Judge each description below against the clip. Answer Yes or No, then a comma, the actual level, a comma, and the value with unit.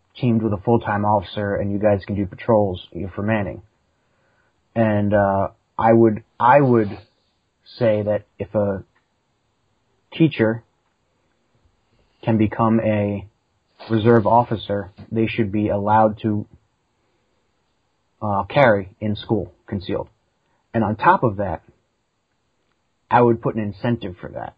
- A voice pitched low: Yes, low, 105 Hz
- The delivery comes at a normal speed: No, slow, 125 wpm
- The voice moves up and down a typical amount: No, narrow, 2.2 semitones